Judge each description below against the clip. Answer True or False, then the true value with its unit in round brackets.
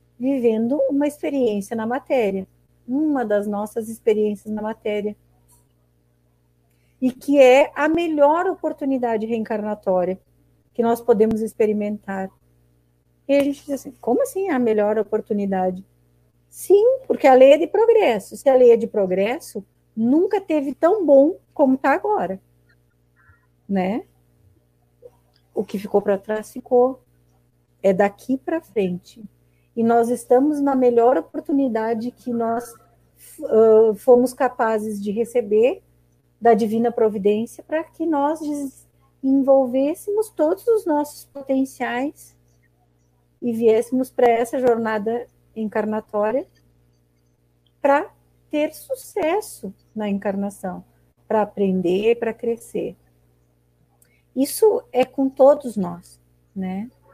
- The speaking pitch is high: True (225 Hz)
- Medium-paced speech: False (115 wpm)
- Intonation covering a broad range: True (6.8 semitones)